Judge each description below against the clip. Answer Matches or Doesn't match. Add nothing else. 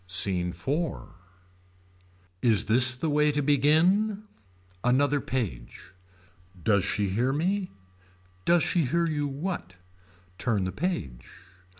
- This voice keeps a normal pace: Doesn't match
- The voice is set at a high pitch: Doesn't match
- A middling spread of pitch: Doesn't match